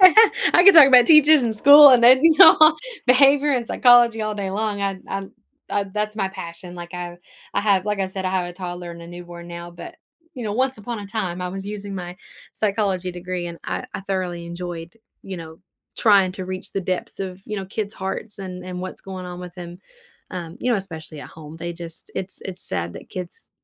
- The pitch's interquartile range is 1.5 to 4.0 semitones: Yes, average, 3.3 semitones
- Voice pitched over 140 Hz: Yes, high, 190 Hz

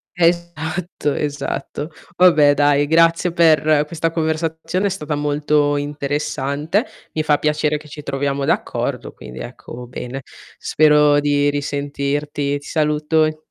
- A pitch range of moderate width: No, narrow, 1.7 semitones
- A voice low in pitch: No, medium, 150 Hz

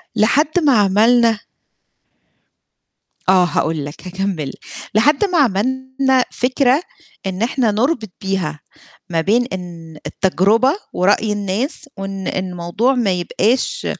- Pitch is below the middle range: No, high, 210 Hz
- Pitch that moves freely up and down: Yes, wide, 5.7 semitones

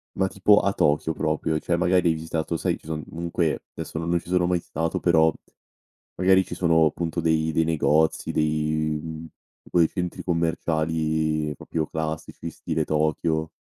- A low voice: Yes, very low, 80 Hz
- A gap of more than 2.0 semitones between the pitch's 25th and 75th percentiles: No, narrow, 1.6 semitones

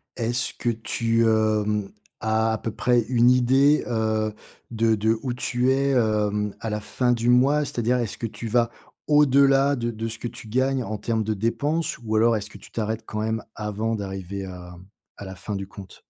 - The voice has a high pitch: No, low, 115 Hz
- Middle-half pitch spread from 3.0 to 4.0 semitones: No, narrow, 2.4 semitones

